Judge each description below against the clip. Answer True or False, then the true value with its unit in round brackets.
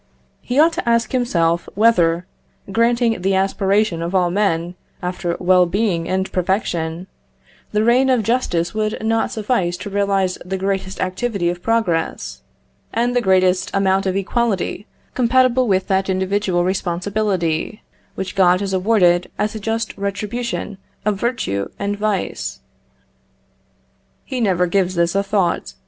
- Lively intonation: False (3.5 semitones)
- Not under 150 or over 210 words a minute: False (140 wpm)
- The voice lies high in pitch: True (195 Hz)